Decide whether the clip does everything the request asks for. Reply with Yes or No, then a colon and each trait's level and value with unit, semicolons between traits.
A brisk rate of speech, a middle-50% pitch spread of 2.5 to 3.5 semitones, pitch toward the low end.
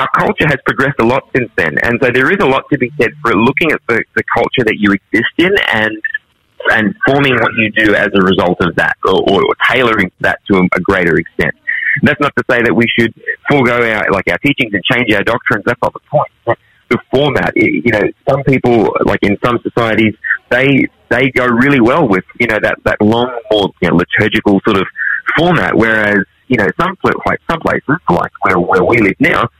Yes: fast, 220 wpm; average, 3.1 semitones; low, 110 Hz